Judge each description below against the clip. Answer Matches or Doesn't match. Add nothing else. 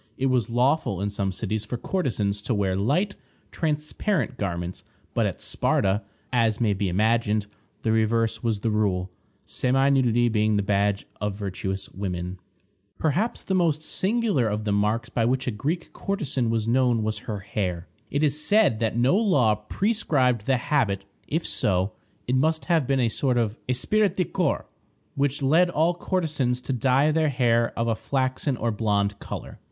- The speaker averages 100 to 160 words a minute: Doesn't match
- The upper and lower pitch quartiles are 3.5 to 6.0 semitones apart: Matches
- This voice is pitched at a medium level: Doesn't match